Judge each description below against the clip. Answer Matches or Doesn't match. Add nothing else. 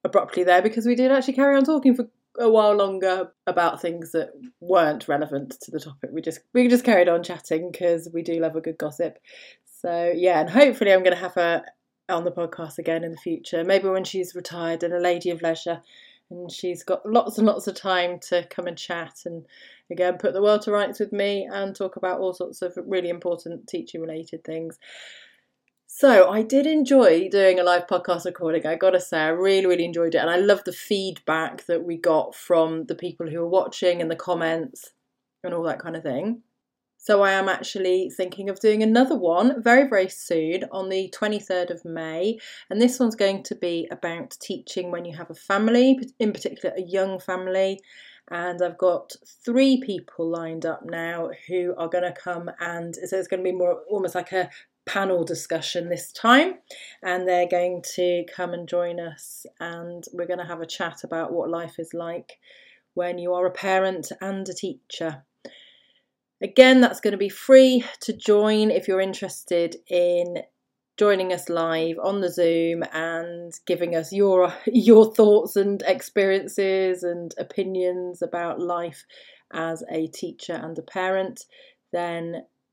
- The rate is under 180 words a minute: Doesn't match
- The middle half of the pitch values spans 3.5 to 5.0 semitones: Doesn't match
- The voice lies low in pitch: Doesn't match